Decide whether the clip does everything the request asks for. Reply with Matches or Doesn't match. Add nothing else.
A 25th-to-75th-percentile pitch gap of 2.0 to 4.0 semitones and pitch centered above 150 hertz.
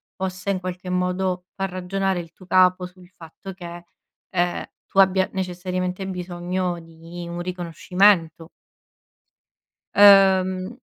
Doesn't match